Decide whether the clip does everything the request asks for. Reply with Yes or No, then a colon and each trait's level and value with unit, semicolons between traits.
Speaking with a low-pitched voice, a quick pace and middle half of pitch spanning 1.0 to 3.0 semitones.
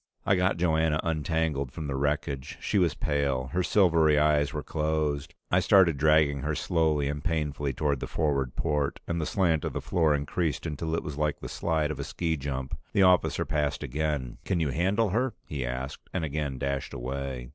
No: very low, 75 Hz; average, 195 wpm; average, 2.7 semitones